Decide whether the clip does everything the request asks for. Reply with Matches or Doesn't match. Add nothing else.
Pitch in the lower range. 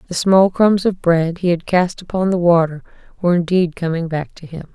Doesn't match